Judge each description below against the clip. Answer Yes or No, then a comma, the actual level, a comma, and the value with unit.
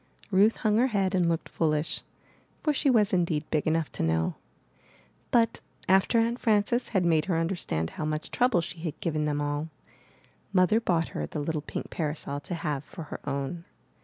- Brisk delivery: No, average, 185 wpm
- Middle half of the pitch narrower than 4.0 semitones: No, average, 5.2 semitones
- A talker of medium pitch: Yes, medium, 165 Hz